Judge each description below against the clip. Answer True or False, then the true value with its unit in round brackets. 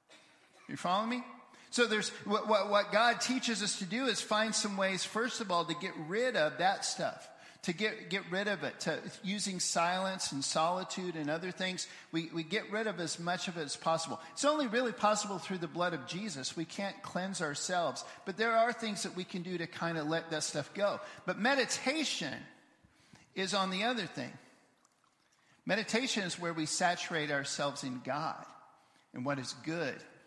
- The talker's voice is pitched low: False (190 Hz)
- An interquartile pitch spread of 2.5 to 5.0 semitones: True (4.5 semitones)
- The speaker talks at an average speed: True (195 wpm)